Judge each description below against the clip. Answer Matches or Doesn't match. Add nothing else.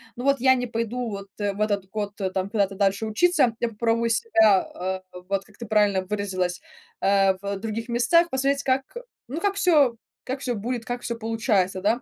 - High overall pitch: Matches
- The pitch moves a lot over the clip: Doesn't match